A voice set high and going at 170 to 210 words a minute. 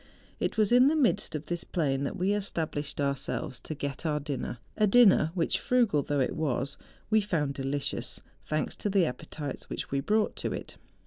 No: medium, 155 Hz; average, 190 wpm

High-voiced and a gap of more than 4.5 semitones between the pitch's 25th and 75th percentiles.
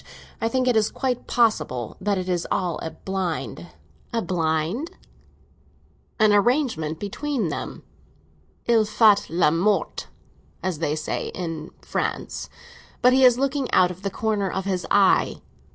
Yes: high, 195 Hz; wide, 5.6 semitones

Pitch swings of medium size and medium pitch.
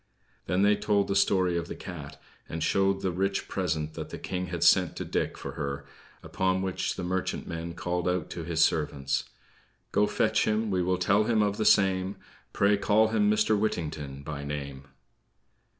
No: average, 3.9 semitones; very low, 90 Hz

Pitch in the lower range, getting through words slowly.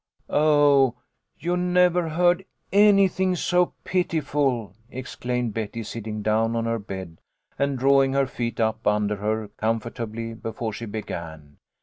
Yes: low, 120 Hz; slow, 130 wpm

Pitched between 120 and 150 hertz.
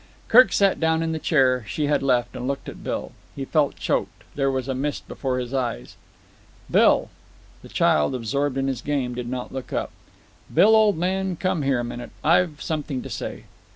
Yes: medium, 140 Hz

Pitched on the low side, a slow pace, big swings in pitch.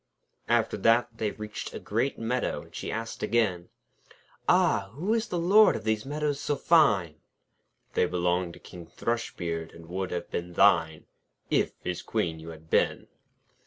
No: low, 105 Hz; average, 160 wpm; wide, 6.3 semitones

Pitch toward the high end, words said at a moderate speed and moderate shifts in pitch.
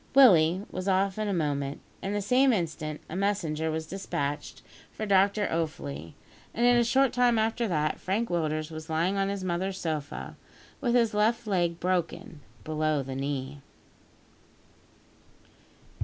No: medium, 180 Hz; average, 150 wpm; average, 4.9 semitones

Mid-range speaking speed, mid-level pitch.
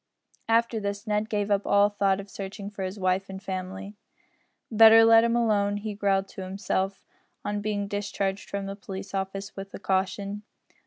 No: average, 175 wpm; high, 200 Hz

